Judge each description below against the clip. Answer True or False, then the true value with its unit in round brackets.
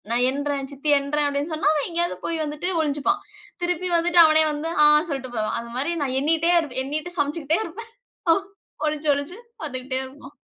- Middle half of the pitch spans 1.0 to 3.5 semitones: True (2.9 semitones)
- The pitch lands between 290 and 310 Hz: True (295 Hz)